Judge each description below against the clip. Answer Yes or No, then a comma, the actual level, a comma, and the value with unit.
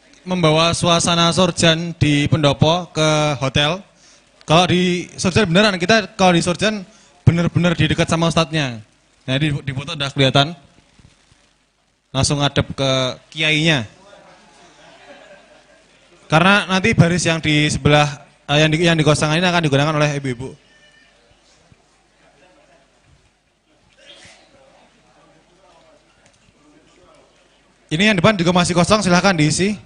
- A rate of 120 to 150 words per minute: No, average, 105 wpm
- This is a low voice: No, medium, 160 Hz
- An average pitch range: Yes, average, 3.3 semitones